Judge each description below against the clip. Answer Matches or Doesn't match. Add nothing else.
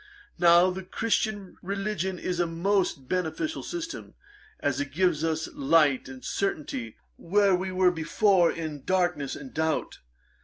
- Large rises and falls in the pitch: Doesn't match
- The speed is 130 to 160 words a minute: Matches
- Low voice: Doesn't match